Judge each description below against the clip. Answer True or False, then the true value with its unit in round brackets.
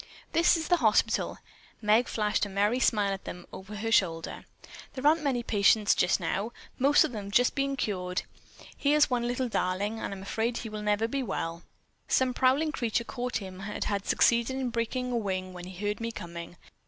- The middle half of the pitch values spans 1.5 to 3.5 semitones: False (4.2 semitones)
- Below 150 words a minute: False (195 wpm)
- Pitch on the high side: True (220 Hz)